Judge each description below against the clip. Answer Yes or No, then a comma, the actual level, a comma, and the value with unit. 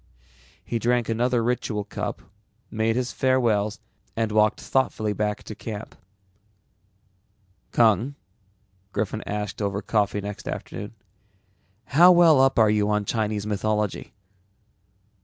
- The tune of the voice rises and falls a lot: No, narrow, 2.5 semitones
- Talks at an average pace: No, slow, 115 wpm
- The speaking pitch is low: Yes, low, 110 Hz